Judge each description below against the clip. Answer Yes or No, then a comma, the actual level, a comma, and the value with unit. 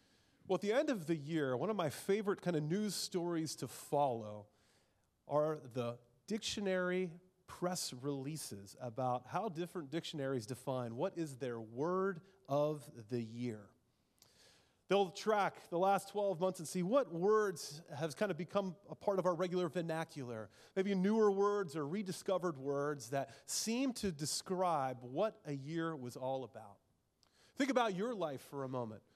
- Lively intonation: Yes, wide, 6.3 semitones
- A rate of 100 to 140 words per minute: No, average, 160 wpm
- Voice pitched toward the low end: No, medium, 165 Hz